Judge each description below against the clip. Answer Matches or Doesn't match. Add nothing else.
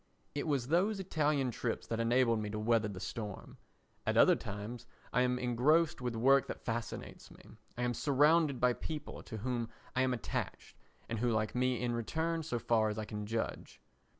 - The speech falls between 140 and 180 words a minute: Doesn't match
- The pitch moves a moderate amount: Matches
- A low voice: Matches